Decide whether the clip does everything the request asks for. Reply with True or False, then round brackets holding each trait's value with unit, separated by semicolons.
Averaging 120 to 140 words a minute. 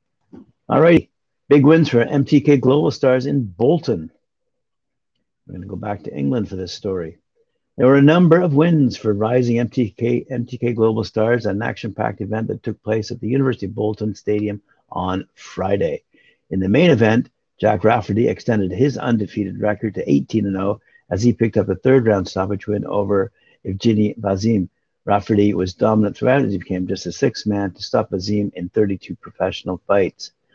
False (175 wpm)